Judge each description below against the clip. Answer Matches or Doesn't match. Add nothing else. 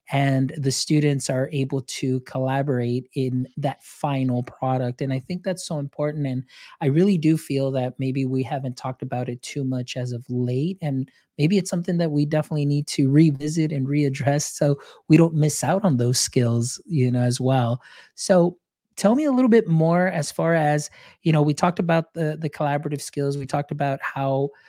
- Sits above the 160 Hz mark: Doesn't match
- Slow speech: Doesn't match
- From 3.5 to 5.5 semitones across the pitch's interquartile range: Doesn't match